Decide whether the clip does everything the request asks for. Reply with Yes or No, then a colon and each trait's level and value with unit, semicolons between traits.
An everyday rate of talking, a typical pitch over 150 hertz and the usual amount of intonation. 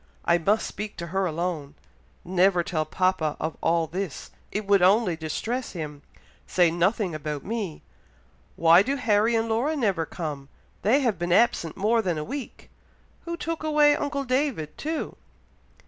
No: average, 160 wpm; high, 190 Hz; wide, 6.1 semitones